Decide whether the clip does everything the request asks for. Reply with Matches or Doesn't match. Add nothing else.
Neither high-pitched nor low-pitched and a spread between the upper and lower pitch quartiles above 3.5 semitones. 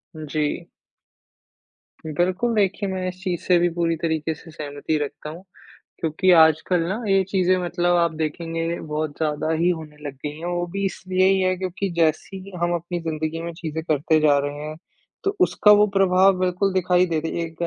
Doesn't match